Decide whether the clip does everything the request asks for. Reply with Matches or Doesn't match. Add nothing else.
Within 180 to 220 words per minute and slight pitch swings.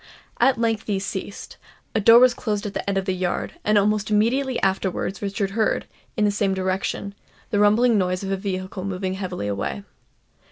Matches